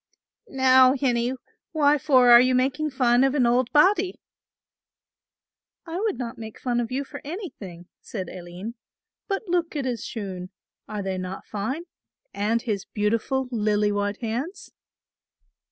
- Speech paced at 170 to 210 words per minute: No, average, 145 wpm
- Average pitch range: Yes, average, 4.9 semitones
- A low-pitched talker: No, high, 245 Hz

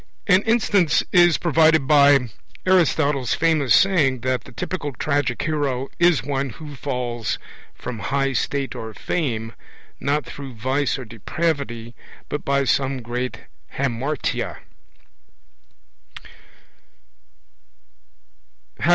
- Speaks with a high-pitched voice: No, medium, 140 Hz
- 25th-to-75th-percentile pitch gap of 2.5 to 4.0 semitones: Yes, average, 3.7 semitones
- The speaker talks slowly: Yes, slow, 100 wpm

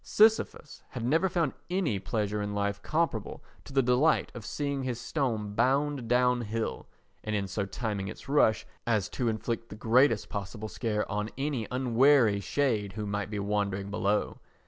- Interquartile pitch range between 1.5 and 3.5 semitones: No, average, 4.6 semitones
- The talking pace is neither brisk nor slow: Yes, average, 170 wpm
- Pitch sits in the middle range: No, low, 115 Hz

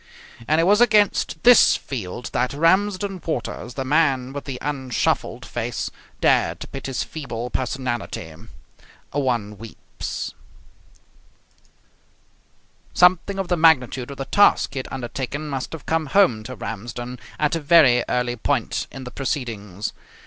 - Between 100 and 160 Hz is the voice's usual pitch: Yes, low, 135 Hz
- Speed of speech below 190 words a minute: Yes, average, 140 wpm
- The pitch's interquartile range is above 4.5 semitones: Yes, average, 4.9 semitones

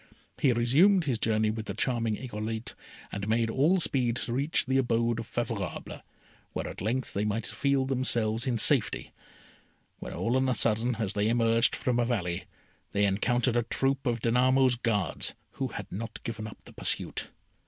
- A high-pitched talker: No, low, 115 Hz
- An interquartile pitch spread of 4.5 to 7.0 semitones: No, average, 2.7 semitones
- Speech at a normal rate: Yes, average, 175 wpm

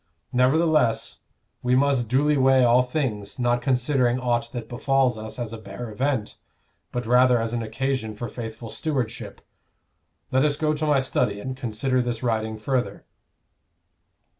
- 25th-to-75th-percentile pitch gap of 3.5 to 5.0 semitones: No, narrow, 2.6 semitones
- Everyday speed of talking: Yes, average, 150 wpm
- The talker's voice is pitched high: No, low, 125 Hz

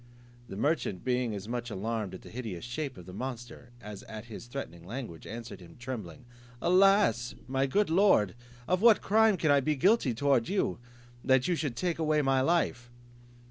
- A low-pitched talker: Yes, low, 125 Hz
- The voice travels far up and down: Yes, wide, 6.0 semitones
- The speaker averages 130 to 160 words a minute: No, average, 180 wpm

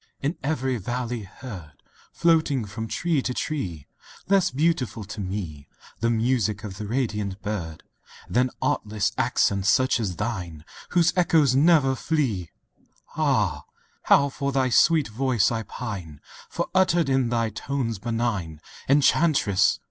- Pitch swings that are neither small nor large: No, wide, 5.7 semitones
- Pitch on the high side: No, low, 120 Hz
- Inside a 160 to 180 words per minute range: No, slow, 135 wpm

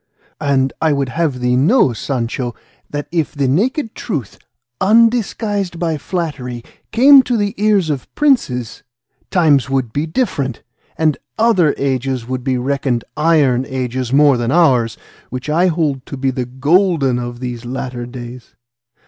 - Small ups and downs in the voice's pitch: No, wide, 5.4 semitones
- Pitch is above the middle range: No, medium, 140 Hz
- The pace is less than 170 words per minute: Yes, average, 150 wpm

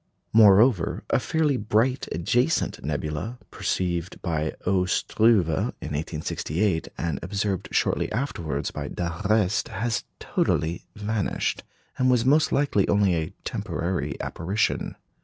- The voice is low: Yes, very low, 95 Hz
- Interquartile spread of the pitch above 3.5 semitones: Yes, average, 5.1 semitones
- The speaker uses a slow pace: Yes, slow, 115 wpm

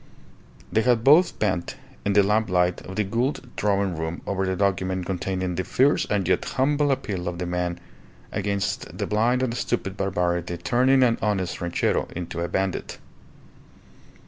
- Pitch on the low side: Yes, very low, 95 Hz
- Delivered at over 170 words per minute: No, average, 160 wpm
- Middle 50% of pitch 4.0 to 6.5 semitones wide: Yes, average, 4.3 semitones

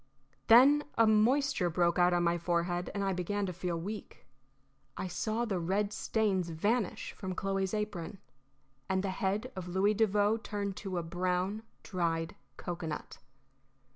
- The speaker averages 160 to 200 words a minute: No, average, 150 wpm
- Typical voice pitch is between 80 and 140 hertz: No, high, 190 Hz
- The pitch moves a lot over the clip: No, average, 3.2 semitones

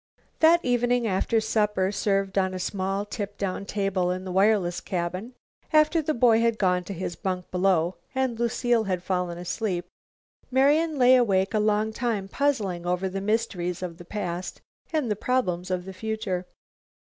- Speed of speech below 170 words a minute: No, average, 175 wpm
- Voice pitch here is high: Yes, high, 200 Hz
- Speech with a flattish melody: No, average, 4.1 semitones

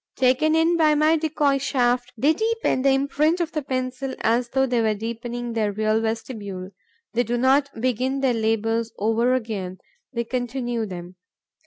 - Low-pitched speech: No, high, 245 Hz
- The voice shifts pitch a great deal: No, average, 3.5 semitones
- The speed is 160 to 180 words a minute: Yes, average, 165 wpm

